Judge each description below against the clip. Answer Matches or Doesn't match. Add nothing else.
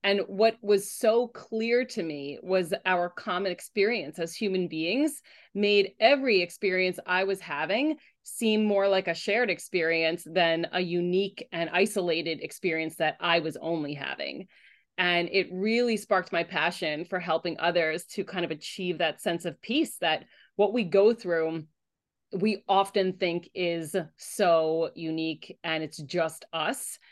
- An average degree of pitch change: Matches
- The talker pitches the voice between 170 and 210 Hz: Matches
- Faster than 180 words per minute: Doesn't match